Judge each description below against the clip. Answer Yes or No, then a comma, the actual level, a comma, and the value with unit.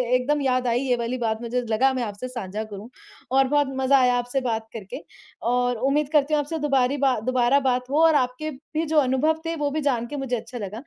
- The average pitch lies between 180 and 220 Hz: No, very high, 255 Hz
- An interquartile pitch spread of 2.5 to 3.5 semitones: Yes, average, 3.1 semitones